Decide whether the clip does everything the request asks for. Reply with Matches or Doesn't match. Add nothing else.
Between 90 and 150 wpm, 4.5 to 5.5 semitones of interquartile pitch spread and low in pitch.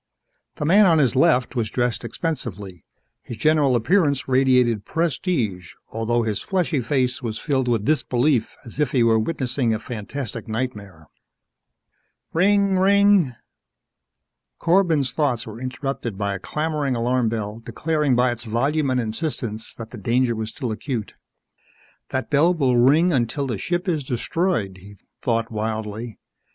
Matches